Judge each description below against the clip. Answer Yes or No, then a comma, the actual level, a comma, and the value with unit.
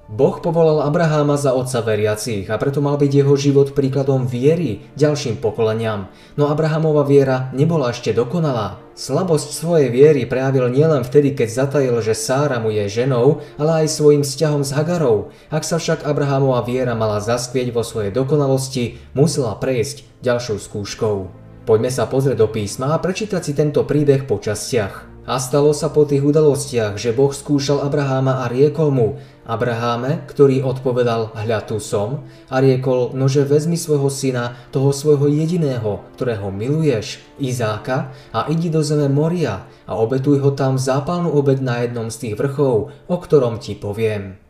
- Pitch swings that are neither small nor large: Yes, average, 3.8 semitones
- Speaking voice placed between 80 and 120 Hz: No, low, 135 Hz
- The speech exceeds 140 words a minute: Yes, average, 160 wpm